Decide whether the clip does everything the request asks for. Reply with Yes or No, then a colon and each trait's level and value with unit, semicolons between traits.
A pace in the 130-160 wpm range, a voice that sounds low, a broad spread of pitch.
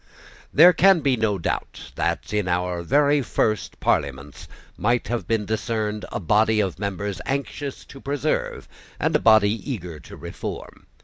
Yes: average, 150 wpm; low, 110 Hz; wide, 6.1 semitones